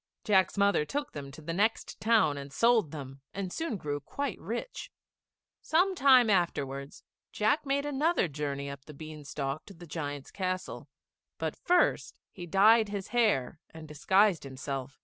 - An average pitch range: No, wide, 7.7 semitones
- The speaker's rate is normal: Yes, average, 160 wpm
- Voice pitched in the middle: Yes, medium, 180 Hz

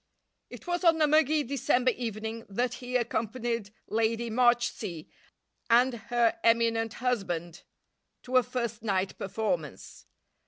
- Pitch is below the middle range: No, high, 235 Hz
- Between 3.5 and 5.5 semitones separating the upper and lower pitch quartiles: No, narrow, 2.5 semitones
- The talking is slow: Yes, slow, 120 wpm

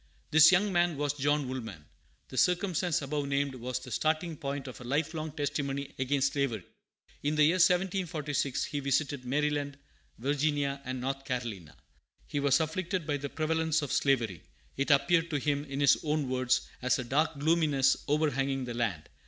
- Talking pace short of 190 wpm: Yes, average, 170 wpm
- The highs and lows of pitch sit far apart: No, average, 2.8 semitones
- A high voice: No, medium, 145 Hz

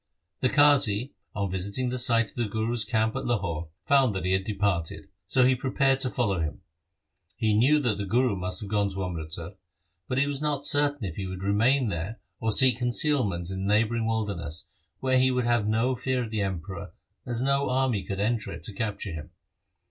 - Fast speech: Yes, fast, 210 wpm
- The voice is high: No, low, 110 Hz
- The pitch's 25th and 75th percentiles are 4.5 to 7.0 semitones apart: Yes, average, 4.8 semitones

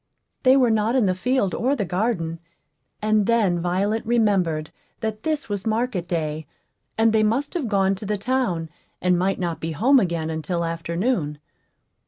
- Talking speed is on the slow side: No, average, 170 wpm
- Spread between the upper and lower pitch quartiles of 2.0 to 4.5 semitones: No, average, 5.1 semitones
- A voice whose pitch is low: No, high, 200 Hz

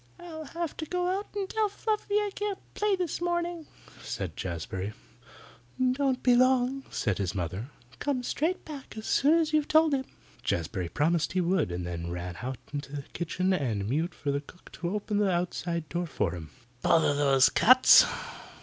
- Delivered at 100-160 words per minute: No, average, 185 wpm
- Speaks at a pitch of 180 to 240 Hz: Yes, medium, 185 Hz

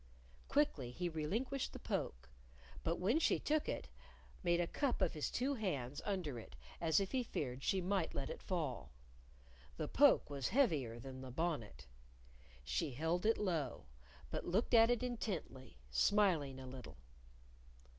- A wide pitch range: Yes, wide, 8.0 semitones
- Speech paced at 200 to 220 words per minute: No, average, 155 wpm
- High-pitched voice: No, medium, 165 Hz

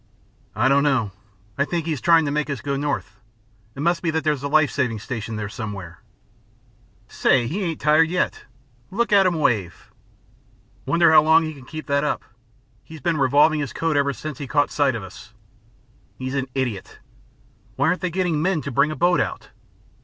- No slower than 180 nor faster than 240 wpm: Yes, average, 200 wpm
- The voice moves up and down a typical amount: Yes, average, 3.6 semitones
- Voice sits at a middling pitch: Yes, medium, 145 Hz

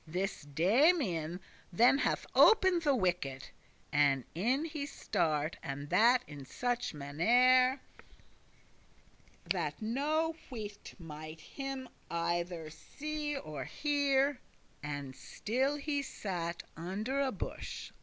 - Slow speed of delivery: Yes, slow, 105 wpm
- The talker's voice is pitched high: Yes, high, 215 Hz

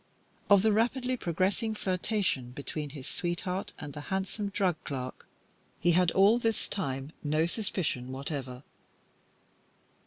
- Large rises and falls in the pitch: Yes, wide, 6.0 semitones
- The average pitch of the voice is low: No, medium, 180 Hz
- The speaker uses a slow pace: Yes, slow, 125 wpm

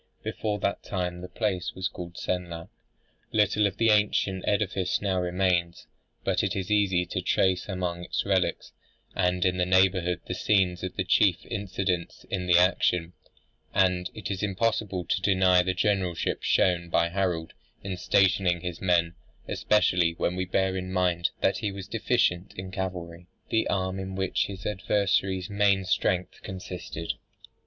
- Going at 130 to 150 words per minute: No, average, 160 wpm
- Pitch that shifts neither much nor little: No, narrow, 1.5 semitones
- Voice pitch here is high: No, very low, 95 Hz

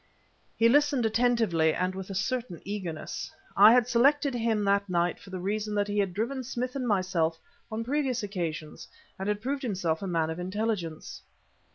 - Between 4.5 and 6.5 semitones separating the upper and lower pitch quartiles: Yes, average, 4.8 semitones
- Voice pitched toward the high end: Yes, high, 205 Hz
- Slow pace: No, average, 180 wpm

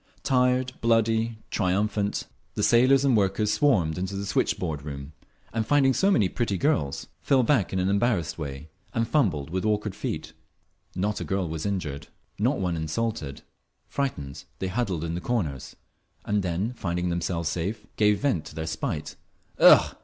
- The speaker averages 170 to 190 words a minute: No, average, 160 wpm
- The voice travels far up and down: Yes, wide, 5.8 semitones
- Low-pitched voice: Yes, low, 100 Hz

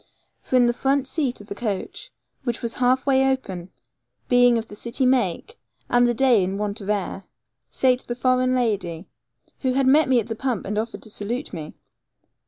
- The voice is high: Yes, high, 240 Hz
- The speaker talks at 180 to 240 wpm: Yes, average, 195 wpm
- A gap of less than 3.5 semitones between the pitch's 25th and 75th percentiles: No, average, 3.9 semitones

